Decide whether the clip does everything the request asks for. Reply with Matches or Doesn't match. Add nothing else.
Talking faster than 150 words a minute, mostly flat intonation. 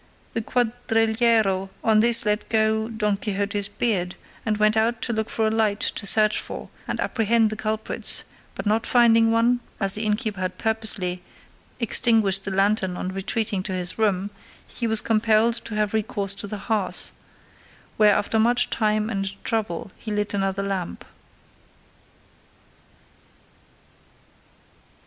Doesn't match